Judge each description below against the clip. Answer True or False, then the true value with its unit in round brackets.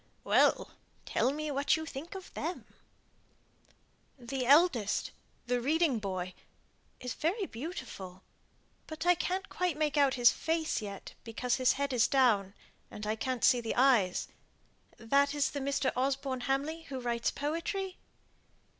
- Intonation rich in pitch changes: False (4.6 semitones)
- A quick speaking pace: False (145 wpm)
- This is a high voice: True (270 Hz)